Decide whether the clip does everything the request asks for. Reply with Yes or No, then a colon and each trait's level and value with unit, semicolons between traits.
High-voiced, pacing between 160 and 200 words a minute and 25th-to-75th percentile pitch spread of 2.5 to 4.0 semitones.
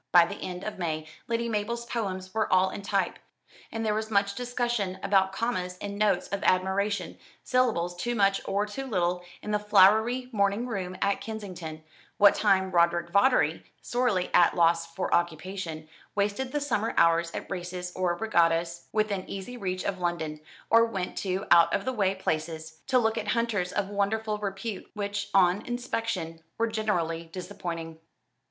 Yes: high, 195 Hz; average, 170 wpm; average, 3.7 semitones